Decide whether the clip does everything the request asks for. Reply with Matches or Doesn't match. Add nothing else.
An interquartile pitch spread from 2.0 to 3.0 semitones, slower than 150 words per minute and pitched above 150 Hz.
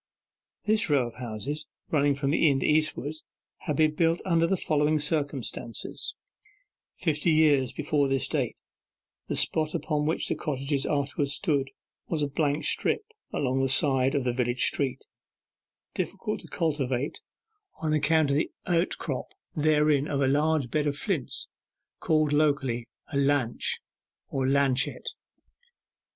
Doesn't match